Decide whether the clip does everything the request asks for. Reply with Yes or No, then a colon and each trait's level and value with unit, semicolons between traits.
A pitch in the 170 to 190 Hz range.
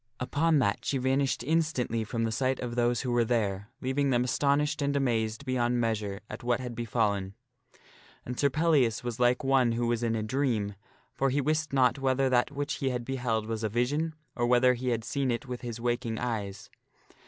No: low, 125 Hz